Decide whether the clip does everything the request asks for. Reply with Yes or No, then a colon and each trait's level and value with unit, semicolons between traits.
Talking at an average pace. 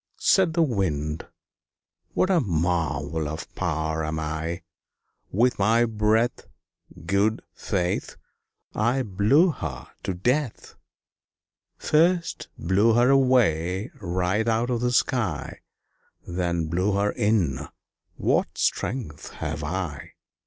No: slow, 110 wpm